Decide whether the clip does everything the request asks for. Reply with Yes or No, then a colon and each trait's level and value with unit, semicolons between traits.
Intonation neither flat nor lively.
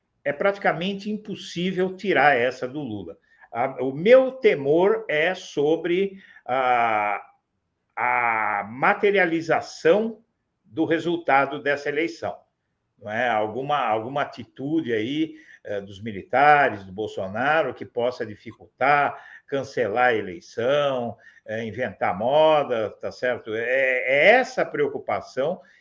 No: wide, 8.6 semitones